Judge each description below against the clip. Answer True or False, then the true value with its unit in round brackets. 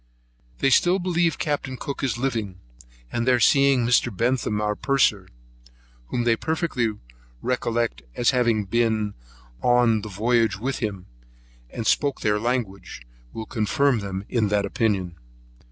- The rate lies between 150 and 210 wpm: False (135 wpm)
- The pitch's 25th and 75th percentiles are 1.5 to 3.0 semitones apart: False (3.5 semitones)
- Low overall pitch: True (115 Hz)